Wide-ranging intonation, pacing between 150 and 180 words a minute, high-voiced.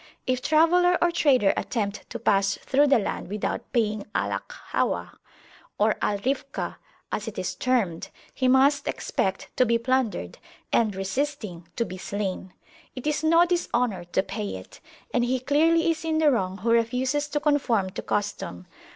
Yes: wide, 6.4 semitones; average, 165 wpm; high, 240 Hz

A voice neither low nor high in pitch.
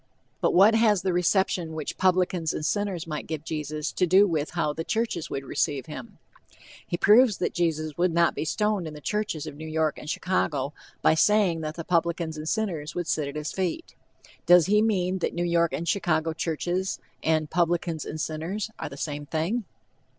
Yes: medium, 170 Hz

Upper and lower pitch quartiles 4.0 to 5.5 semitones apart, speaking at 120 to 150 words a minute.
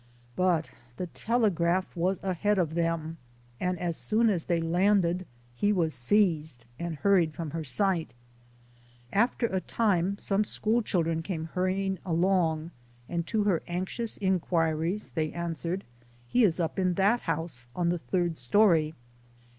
No: average, 3.1 semitones; average, 145 wpm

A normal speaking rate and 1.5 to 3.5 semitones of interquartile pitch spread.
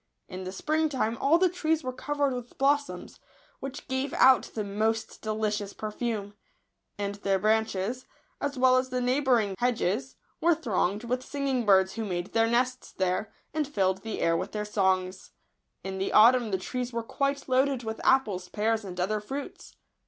No: average, 180 wpm; average, 4.6 semitones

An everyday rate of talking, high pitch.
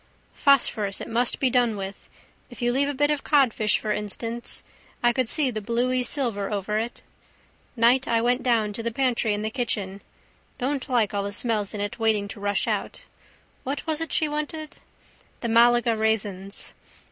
Yes: average, 180 wpm; high, 235 Hz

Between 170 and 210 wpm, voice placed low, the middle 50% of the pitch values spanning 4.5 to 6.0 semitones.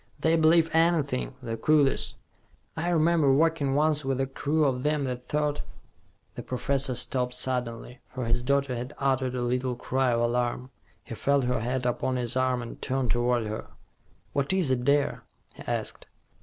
No: average, 175 wpm; low, 130 Hz; average, 2.9 semitones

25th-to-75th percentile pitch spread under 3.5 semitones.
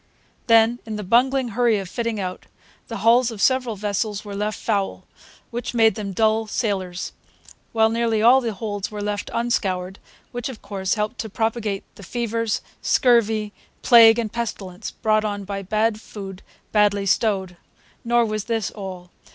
Yes: narrow, 2.5 semitones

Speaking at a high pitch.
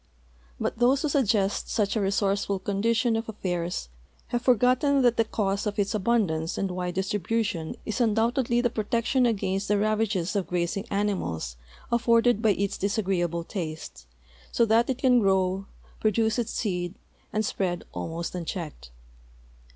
Yes: high, 205 Hz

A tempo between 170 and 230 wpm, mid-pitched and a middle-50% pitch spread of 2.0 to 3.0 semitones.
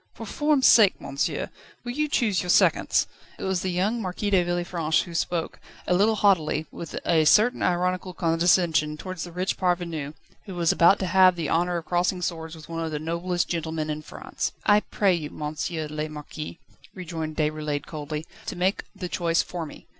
Yes: average, 190 wpm; medium, 175 Hz; average, 2.7 semitones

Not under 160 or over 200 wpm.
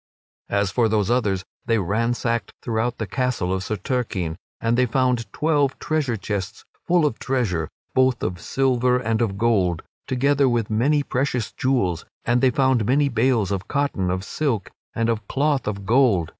Yes: average, 170 wpm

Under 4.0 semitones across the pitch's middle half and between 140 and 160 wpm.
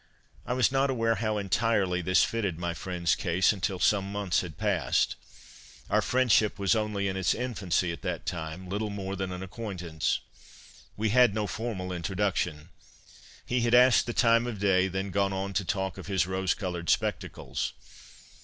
No: average, 3.1 semitones; average, 175 wpm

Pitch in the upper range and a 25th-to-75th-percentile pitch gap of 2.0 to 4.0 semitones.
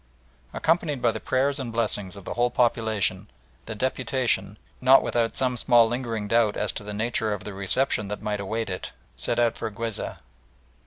No: low, 115 Hz; average, 2.9 semitones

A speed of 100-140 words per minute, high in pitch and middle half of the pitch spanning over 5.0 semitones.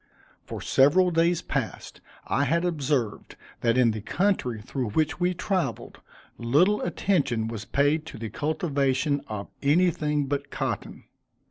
No: slow, 135 wpm; medium, 145 Hz; wide, 5.6 semitones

